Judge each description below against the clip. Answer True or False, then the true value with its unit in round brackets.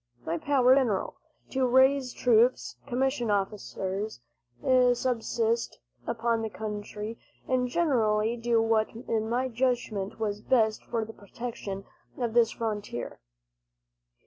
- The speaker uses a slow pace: True (120 wpm)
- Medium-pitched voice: False (230 Hz)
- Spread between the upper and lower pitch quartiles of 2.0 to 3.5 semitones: True (2.7 semitones)